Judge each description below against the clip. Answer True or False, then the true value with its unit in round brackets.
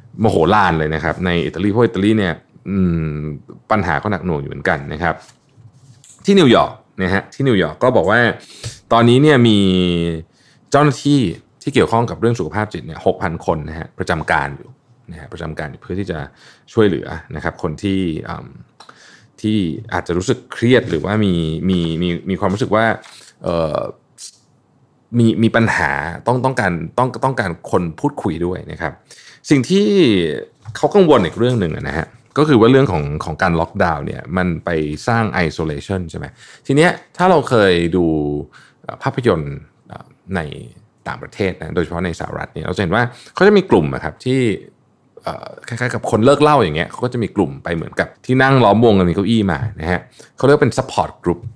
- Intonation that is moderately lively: False (6.1 semitones)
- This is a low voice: True (105 Hz)